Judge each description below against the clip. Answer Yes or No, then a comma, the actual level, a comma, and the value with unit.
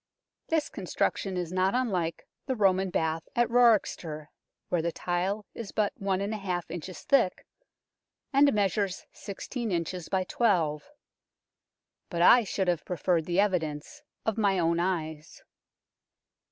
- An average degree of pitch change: Yes, average, 3.4 semitones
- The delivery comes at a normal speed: No, slow, 130 wpm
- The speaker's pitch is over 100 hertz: Yes, medium, 185 Hz